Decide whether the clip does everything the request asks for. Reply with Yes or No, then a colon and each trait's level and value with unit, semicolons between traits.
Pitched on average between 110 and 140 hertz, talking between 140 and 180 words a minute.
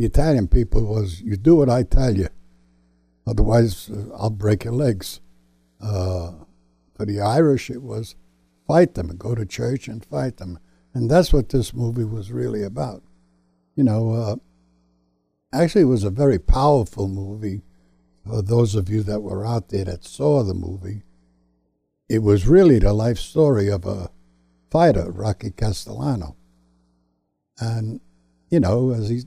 No: low, 100 Hz; average, 155 wpm